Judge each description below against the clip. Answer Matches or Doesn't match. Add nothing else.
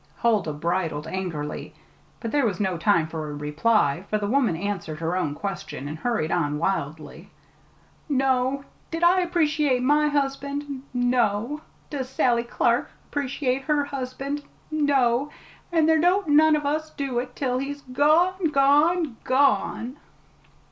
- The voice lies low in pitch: Doesn't match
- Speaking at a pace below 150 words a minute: Matches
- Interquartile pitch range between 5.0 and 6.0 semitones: Doesn't match